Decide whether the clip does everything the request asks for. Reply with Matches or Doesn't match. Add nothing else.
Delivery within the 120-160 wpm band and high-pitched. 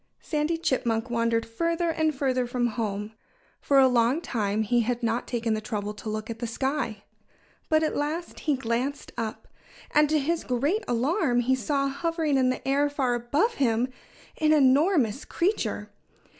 Doesn't match